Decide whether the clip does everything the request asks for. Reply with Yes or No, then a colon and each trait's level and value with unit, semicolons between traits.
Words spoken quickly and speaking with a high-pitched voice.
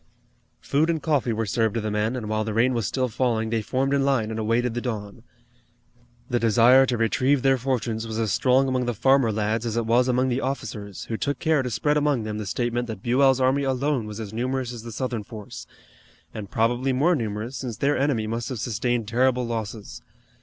No: fast, 215 wpm; low, 120 Hz